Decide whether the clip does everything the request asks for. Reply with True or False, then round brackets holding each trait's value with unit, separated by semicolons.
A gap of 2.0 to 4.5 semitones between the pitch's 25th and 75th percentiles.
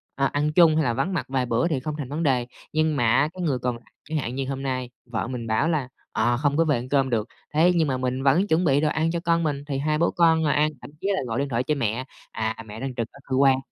True (3.9 semitones)